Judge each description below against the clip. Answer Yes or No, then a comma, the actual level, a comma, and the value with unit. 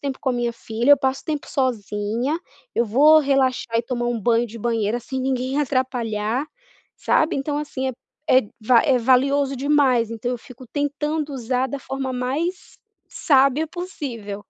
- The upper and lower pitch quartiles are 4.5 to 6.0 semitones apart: No, average, 3.1 semitones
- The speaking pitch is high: Yes, very high, 260 Hz